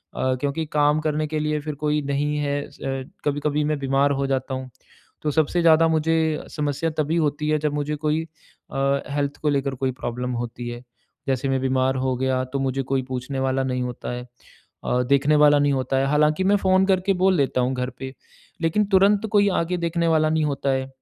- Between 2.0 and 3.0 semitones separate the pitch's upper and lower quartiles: Yes, narrow, 2.6 semitones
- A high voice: No, medium, 145 Hz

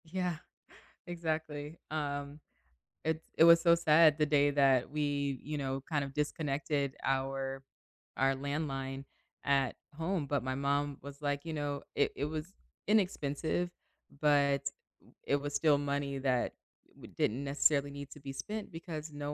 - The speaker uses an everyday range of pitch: No, narrow, 2.0 semitones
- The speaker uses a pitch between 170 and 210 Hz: No, medium, 145 Hz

